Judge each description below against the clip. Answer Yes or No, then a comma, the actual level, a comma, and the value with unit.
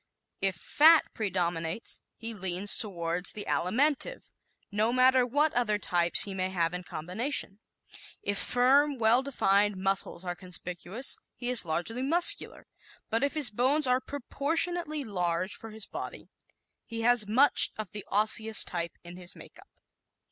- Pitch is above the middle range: Yes, high, 215 Hz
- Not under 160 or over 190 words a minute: No, average, 145 wpm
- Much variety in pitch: Yes, wide, 5.9 semitones